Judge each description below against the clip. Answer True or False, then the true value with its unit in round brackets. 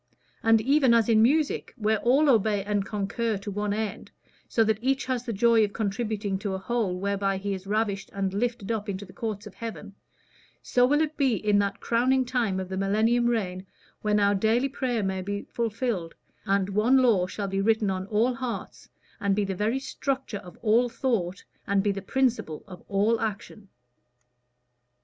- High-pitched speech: True (215 Hz)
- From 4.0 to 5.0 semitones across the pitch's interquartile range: False (3.2 semitones)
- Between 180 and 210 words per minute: True (190 wpm)